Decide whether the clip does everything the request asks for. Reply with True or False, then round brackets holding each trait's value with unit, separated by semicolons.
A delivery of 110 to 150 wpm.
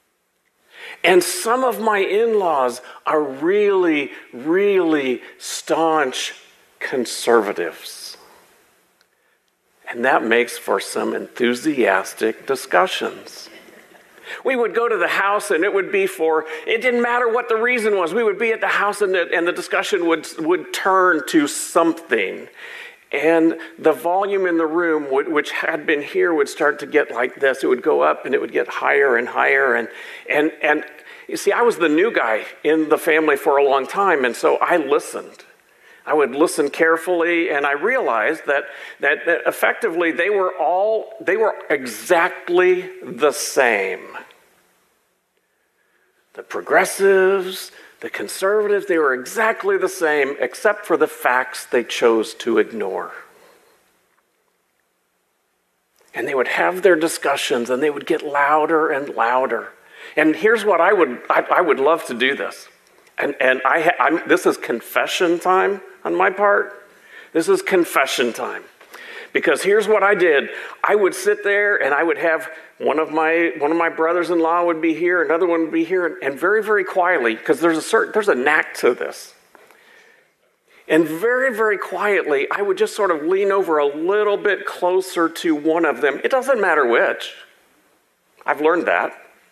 False (165 wpm)